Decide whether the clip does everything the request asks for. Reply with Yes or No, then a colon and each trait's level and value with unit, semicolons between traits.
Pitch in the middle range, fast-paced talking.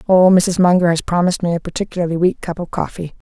Yes: medium, 175 Hz; fast, 215 wpm